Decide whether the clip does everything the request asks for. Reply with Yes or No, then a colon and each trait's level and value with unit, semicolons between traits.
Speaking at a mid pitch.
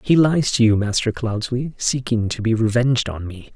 No: low, 115 Hz